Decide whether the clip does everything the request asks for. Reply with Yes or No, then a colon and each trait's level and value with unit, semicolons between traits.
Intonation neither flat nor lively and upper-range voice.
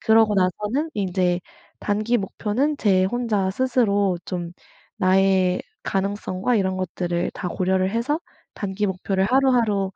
Yes: average, 3.2 semitones; high, 195 Hz